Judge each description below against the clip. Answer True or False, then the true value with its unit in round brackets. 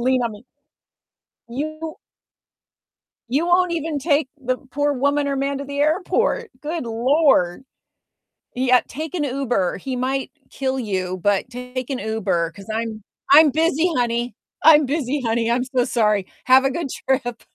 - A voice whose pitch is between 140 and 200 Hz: False (260 Hz)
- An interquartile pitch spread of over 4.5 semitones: False (3.7 semitones)